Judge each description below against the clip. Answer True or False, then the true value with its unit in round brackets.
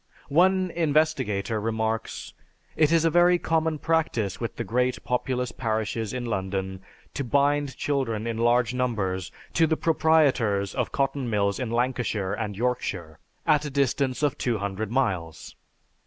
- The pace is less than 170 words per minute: True (140 wpm)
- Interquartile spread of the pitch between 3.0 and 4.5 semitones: False (5.3 semitones)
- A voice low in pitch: True (125 Hz)